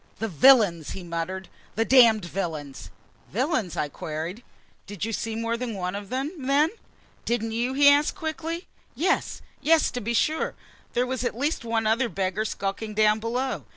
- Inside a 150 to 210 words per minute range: Yes, average, 170 wpm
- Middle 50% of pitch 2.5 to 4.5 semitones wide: No, average, 5.3 semitones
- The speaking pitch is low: No, high, 225 Hz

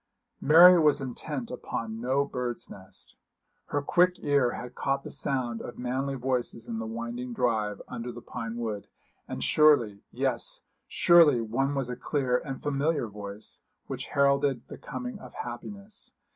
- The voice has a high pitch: No, low, 125 Hz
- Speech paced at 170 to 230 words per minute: No, average, 155 wpm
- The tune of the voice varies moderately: Yes, average, 3.4 semitones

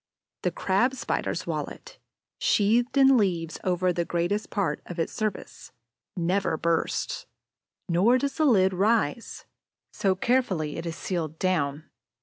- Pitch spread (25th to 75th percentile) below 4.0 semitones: No, average, 5.0 semitones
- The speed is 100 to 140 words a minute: Yes, slow, 135 wpm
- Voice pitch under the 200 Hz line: Yes, medium, 185 Hz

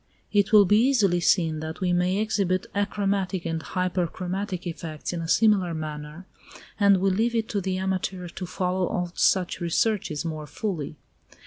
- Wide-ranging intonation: No, average, 2.8 semitones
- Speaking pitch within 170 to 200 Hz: Yes, medium, 185 Hz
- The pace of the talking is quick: No, average, 160 wpm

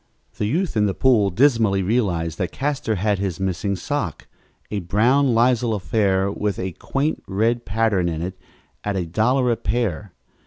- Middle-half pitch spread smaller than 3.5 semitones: No, average, 4.0 semitones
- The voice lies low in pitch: Yes, low, 105 Hz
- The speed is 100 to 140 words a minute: No, average, 165 wpm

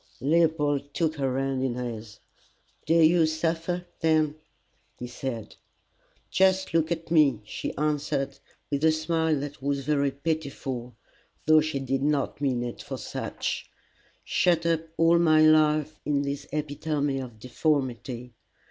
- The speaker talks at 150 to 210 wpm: No, average, 140 wpm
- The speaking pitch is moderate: Yes, medium, 145 Hz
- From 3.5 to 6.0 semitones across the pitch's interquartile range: No, average, 2.9 semitones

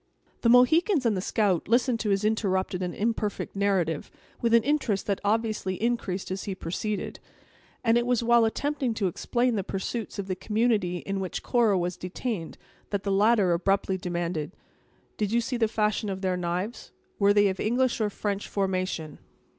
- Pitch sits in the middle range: No, high, 205 Hz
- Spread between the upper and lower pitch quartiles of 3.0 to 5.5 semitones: Yes, average, 3.7 semitones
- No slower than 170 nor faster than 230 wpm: Yes, average, 180 wpm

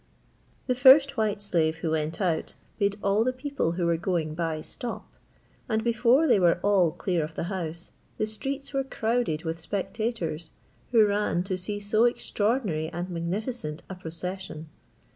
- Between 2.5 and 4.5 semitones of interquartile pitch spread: No, average, 5.2 semitones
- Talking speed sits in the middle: Yes, average, 160 wpm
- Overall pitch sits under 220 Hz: Yes, high, 190 Hz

